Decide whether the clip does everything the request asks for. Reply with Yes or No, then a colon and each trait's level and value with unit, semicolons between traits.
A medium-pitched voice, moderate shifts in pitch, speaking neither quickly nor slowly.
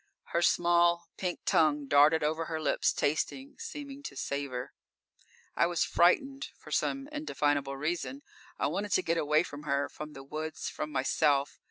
Yes: medium, 160 Hz; average, 3.5 semitones; average, 160 wpm